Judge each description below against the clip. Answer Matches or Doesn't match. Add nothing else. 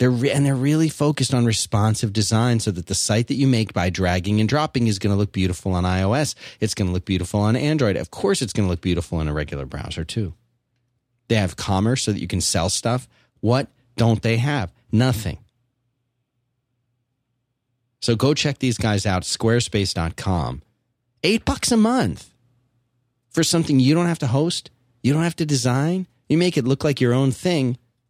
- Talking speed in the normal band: Matches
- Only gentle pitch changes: Doesn't match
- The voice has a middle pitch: Doesn't match